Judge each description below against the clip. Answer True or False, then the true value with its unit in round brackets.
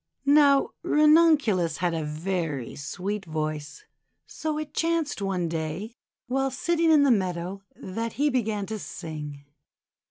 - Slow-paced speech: True (130 wpm)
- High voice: True (200 Hz)